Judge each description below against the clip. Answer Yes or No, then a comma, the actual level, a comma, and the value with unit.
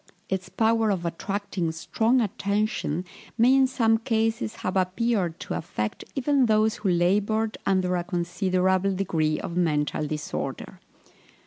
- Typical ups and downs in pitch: Yes, average, 4.2 semitones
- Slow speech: Yes, slow, 130 wpm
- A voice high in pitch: Yes, high, 195 Hz